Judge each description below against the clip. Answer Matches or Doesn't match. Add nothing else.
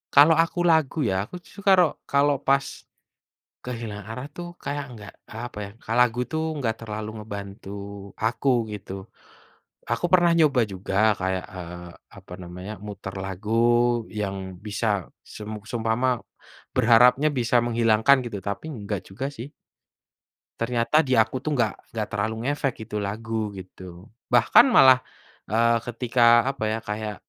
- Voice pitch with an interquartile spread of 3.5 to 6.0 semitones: Matches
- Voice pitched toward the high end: Doesn't match